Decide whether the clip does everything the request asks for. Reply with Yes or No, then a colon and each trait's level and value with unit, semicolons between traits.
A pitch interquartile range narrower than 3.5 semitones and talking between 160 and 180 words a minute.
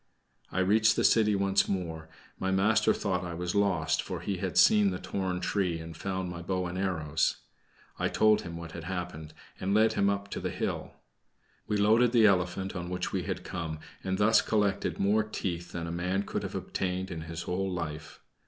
No: average, 2.8 semitones; average, 200 wpm